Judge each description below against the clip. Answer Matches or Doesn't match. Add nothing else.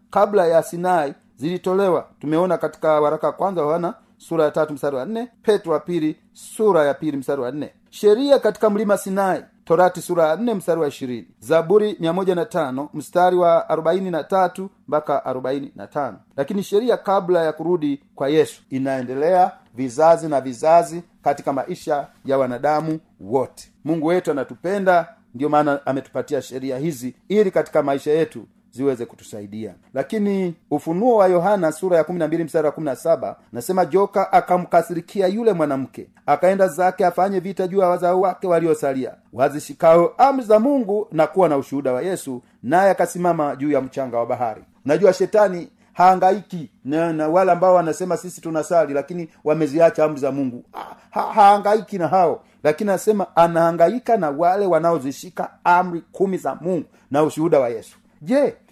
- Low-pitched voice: Doesn't match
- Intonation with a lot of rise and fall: Doesn't match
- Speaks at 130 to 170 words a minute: Matches